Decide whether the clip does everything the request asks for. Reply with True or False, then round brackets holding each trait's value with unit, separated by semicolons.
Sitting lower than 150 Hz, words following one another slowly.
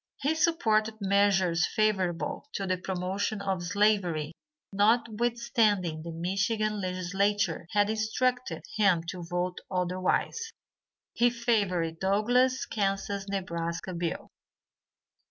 False (200 Hz; 100 wpm)